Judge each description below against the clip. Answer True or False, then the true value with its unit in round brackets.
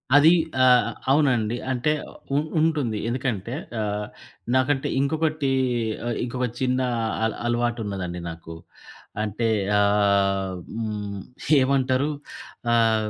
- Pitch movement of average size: True (4.2 semitones)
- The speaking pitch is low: True (120 Hz)